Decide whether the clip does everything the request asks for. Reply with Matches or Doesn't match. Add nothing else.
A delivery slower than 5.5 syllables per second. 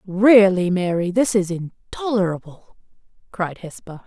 Matches